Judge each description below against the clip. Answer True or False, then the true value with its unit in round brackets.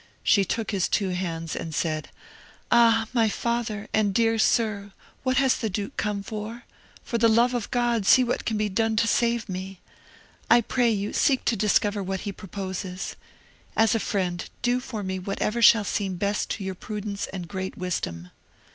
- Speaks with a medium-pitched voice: False (210 Hz)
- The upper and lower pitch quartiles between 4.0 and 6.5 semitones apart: False (3.3 semitones)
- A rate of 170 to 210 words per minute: True (180 wpm)